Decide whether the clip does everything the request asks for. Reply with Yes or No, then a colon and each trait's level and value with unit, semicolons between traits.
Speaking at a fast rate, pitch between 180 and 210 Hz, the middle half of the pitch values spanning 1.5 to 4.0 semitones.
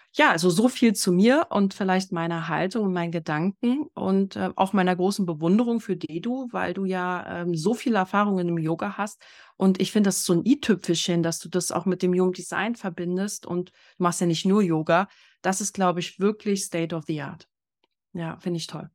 Yes: fast, 215 wpm; medium, 185 Hz; narrow, 2.6 semitones